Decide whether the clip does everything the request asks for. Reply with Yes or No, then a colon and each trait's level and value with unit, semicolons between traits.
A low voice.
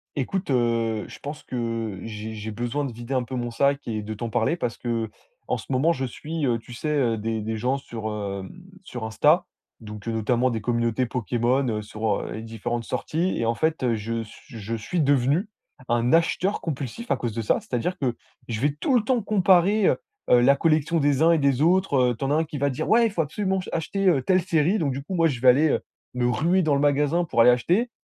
Yes: low, 130 Hz